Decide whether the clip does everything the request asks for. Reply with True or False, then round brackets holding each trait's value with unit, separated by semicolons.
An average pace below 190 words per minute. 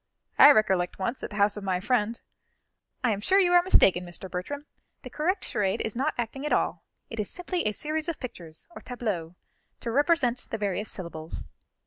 False (200 wpm)